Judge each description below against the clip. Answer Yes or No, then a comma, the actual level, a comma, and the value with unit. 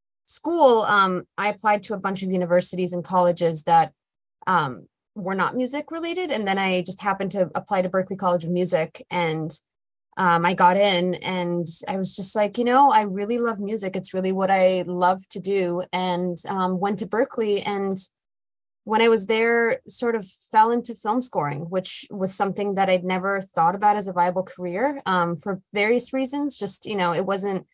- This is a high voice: Yes, high, 195 Hz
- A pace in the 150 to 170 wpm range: No, average, 195 wpm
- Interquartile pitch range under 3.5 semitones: Yes, average, 2.8 semitones